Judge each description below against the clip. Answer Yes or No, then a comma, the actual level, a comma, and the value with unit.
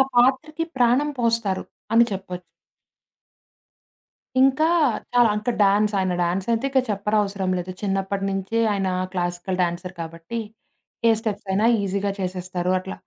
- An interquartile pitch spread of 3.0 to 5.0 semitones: Yes, average, 3.7 semitones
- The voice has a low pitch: No, high, 195 Hz